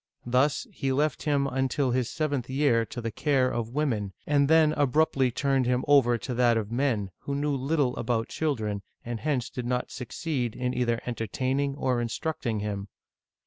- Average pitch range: Yes, average, 3.1 semitones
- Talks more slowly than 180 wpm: No, average, 185 wpm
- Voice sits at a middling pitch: No, low, 130 Hz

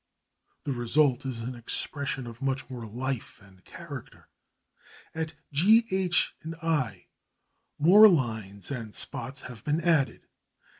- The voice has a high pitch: No, low, 135 Hz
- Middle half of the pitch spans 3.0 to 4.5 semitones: No, wide, 5.6 semitones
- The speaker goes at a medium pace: No, slow, 120 wpm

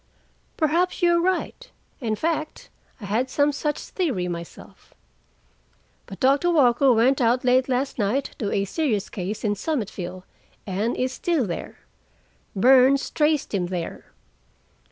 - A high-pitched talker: Yes, very high, 255 Hz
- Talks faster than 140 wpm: No, slow, 135 wpm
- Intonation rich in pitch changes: Yes, wide, 6.5 semitones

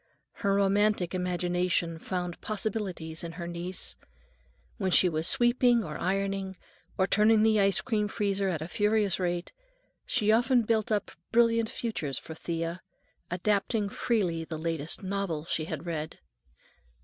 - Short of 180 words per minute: Yes, average, 140 wpm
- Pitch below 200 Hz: Yes, high, 190 Hz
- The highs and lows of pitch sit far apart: No, average, 3.8 semitones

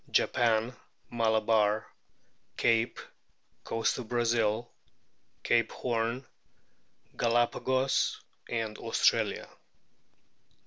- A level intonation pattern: Yes, narrow, 1.3 semitones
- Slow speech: Yes, slow, 55 wpm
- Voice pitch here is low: Yes, low, 115 Hz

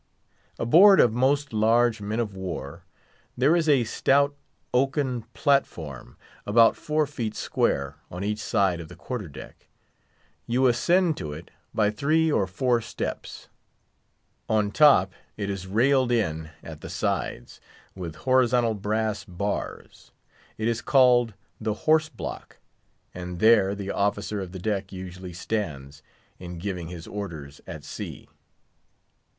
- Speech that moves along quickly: No, slow, 135 wpm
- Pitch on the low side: Yes, low, 110 Hz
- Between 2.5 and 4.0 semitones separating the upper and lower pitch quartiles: No, average, 5.3 semitones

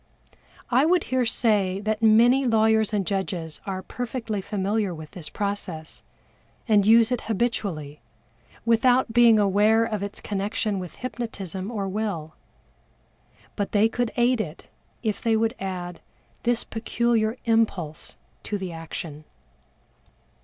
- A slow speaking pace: Yes, slow, 130 wpm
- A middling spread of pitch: Yes, average, 3.2 semitones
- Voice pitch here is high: Yes, high, 215 Hz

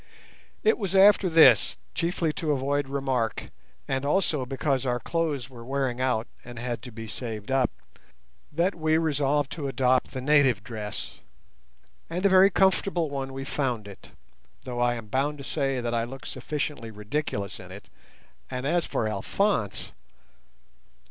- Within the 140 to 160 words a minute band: Yes, average, 155 wpm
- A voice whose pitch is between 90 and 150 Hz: Yes, low, 135 Hz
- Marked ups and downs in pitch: No, average, 4.3 semitones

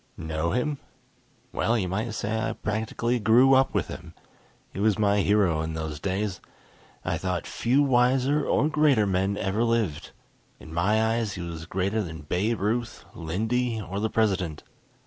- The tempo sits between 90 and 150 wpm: No, average, 165 wpm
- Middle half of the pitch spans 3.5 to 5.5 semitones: Yes, average, 4.2 semitones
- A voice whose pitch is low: Yes, low, 105 Hz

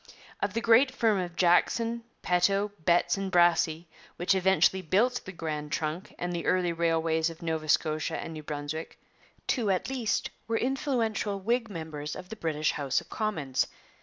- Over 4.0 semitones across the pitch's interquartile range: Yes, average, 5.0 semitones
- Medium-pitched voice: Yes, medium, 175 Hz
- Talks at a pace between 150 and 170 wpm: Yes, average, 165 wpm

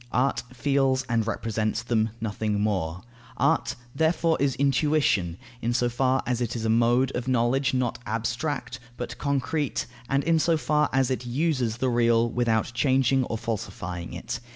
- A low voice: Yes, low, 120 Hz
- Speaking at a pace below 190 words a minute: Yes, average, 160 wpm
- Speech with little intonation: No, average, 3.1 semitones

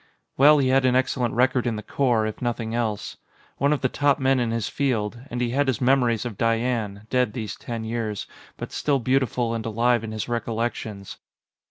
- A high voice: No, low, 120 Hz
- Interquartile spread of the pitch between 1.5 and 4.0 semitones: Yes, narrow, 2.5 semitones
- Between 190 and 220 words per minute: Yes, average, 200 wpm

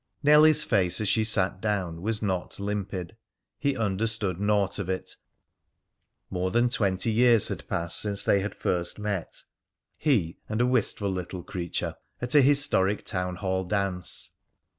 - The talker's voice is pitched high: No, low, 100 Hz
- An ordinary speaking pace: Yes, average, 150 wpm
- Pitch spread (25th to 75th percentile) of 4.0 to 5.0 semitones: No, average, 3.4 semitones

